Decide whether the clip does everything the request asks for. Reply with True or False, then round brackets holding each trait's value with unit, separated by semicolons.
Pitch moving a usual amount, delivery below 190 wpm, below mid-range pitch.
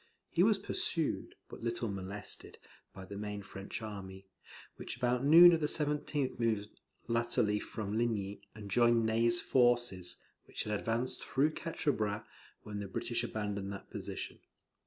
True (3.4 semitones; 150 wpm; 115 Hz)